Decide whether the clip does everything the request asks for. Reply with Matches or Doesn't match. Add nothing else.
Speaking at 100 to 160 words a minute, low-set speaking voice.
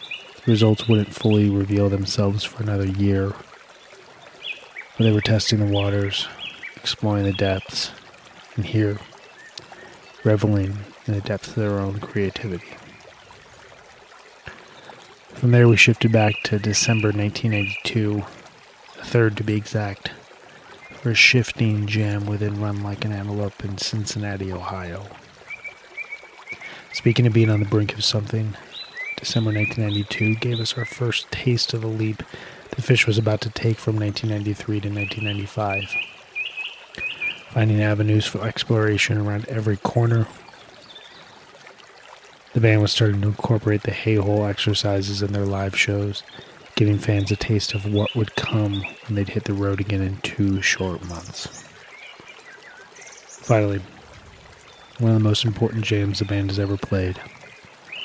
Matches